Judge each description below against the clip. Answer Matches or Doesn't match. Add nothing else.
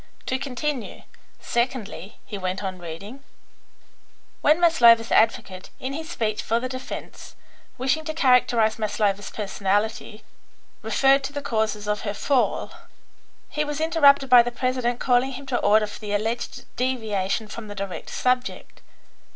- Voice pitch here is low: Doesn't match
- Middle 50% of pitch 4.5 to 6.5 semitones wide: Doesn't match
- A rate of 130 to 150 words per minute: Matches